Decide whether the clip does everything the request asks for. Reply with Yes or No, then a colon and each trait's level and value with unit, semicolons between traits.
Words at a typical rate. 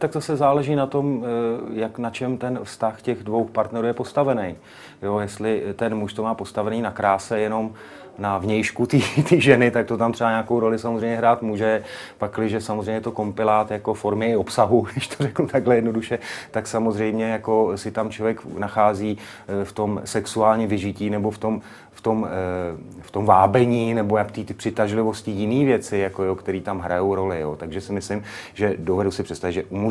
No: fast, 185 wpm